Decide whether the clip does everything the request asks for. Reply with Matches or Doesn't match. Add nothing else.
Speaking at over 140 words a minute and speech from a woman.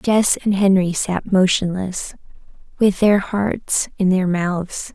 Doesn't match